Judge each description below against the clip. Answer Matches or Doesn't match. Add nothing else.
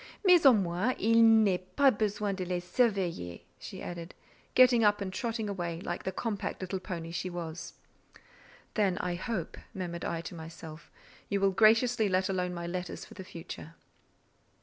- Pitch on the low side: Doesn't match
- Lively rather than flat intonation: Doesn't match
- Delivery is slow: Doesn't match